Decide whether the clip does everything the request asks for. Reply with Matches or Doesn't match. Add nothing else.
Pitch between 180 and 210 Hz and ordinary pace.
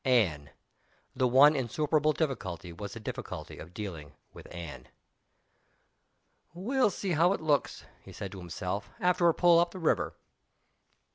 Doesn't match